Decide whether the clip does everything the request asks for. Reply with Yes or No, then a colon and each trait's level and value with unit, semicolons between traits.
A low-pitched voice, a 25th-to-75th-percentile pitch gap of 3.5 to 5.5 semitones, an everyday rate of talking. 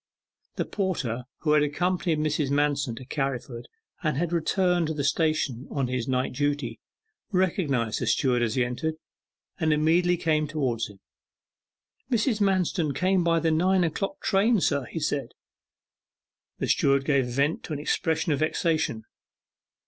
No: medium, 150 Hz; average, 4.2 semitones; average, 150 wpm